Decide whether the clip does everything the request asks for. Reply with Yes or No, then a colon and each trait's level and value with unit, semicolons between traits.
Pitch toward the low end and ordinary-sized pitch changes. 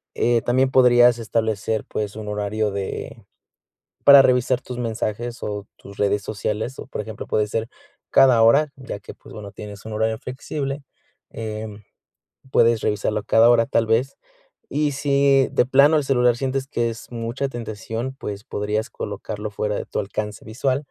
Yes: low, 115 Hz; average, 3.6 semitones